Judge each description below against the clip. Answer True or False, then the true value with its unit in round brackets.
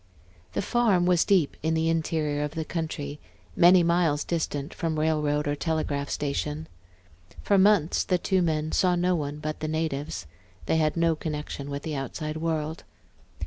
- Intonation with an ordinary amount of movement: False (2.3 semitones)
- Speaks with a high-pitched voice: False (160 Hz)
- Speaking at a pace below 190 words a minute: True (165 wpm)